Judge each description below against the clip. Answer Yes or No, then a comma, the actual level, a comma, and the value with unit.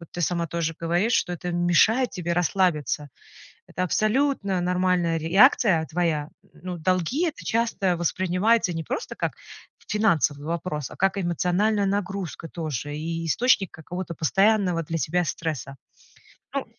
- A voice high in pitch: No, medium, 175 Hz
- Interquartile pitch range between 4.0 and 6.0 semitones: No, average, 3.2 semitones